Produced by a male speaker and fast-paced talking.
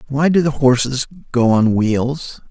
No: male; average, 170 wpm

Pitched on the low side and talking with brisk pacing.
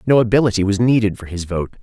Yes: low, 105 Hz; fast, 230 wpm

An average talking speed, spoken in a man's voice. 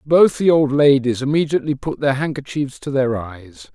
Yes: average, 175 wpm; male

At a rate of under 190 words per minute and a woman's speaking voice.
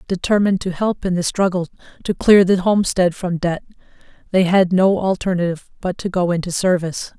Yes: average, 175 wpm; female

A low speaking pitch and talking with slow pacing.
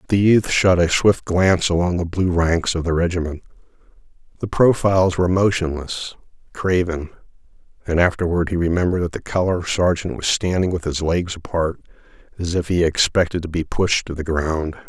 No: very low, 85 Hz; average, 170 wpm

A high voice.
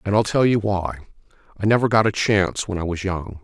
No: low, 100 Hz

